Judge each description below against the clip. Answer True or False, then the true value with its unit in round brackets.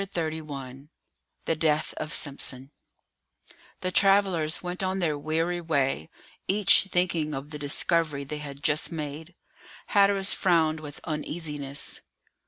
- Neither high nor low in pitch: True (155 Hz)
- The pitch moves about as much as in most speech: True (3.3 semitones)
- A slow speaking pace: True (125 wpm)